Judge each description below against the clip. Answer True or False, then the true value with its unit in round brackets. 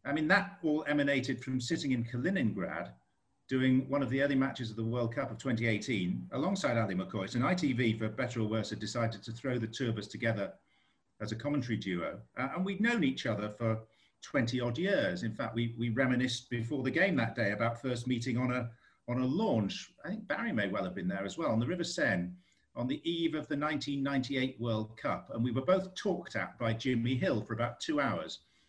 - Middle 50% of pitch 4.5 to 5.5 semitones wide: False (3.2 semitones)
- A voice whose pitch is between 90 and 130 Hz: True (120 Hz)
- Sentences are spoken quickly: True (225 wpm)